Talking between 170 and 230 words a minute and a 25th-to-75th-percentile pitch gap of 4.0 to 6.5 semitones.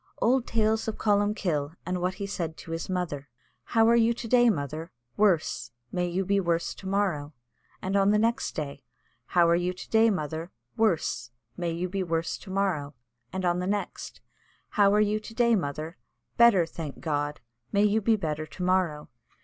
Yes: average, 190 wpm; average, 4.4 semitones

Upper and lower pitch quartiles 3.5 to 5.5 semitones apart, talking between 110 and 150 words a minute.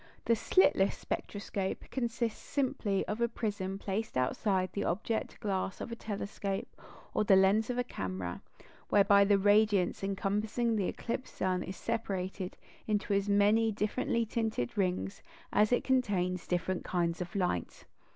No: average, 2.8 semitones; average, 145 wpm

